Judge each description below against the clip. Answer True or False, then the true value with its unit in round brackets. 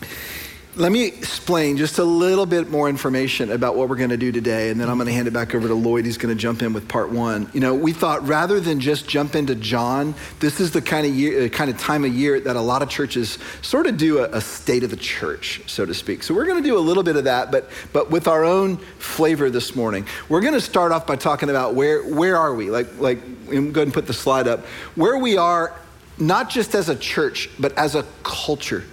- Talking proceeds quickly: True (245 wpm)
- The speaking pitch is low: False (145 Hz)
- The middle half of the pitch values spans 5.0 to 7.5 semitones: True (5.4 semitones)